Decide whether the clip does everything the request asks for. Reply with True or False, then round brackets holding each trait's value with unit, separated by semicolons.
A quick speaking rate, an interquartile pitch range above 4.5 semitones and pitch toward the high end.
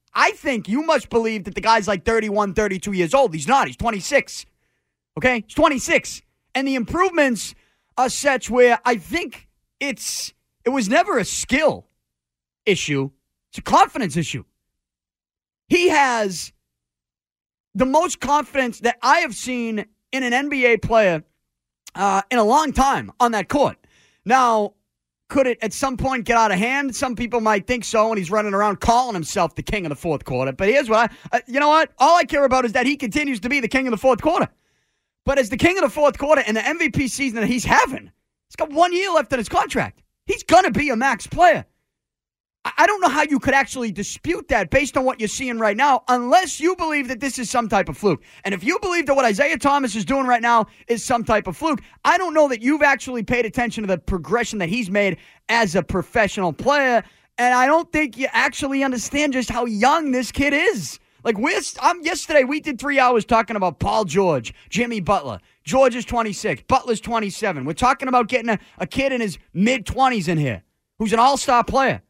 True (210 wpm; 5.0 semitones; 245 Hz)